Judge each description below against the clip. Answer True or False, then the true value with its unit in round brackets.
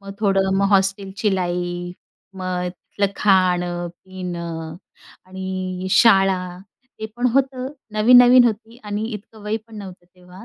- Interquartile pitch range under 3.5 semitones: True (2.9 semitones)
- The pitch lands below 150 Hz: False (190 Hz)